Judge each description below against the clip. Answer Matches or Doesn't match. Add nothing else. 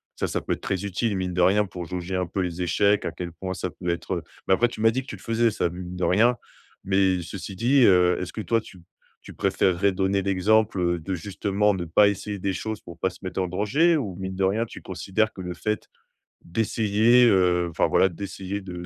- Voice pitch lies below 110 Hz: Matches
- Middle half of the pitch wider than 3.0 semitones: Doesn't match